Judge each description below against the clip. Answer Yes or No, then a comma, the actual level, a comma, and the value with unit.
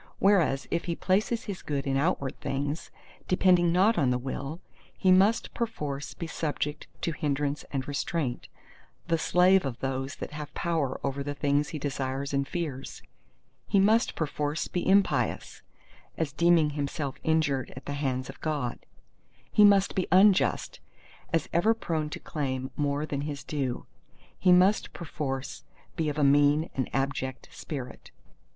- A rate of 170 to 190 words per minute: No, average, 155 wpm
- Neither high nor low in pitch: Yes, medium, 150 Hz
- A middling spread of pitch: Yes, average, 3.9 semitones